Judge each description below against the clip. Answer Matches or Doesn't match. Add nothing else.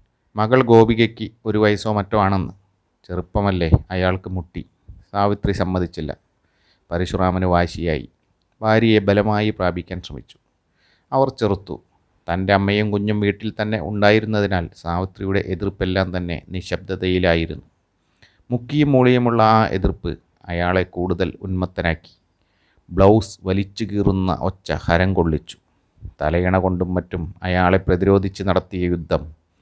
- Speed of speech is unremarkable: Matches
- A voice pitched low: Matches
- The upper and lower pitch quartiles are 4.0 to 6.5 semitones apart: Doesn't match